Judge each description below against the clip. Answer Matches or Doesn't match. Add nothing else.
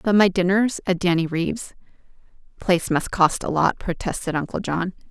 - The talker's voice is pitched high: Doesn't match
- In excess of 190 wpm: Doesn't match